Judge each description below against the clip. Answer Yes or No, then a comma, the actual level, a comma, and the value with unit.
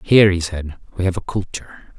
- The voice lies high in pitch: No, very low, 90 Hz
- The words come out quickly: Yes, fast, 210 wpm